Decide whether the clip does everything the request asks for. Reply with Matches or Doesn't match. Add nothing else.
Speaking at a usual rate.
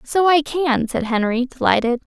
Matches